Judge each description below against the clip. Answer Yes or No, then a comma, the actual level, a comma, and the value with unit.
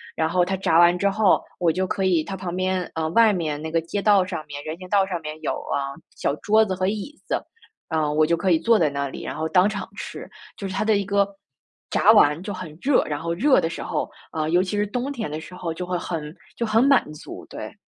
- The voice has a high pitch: No, medium, 180 Hz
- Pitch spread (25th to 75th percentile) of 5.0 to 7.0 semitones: No, average, 4.0 semitones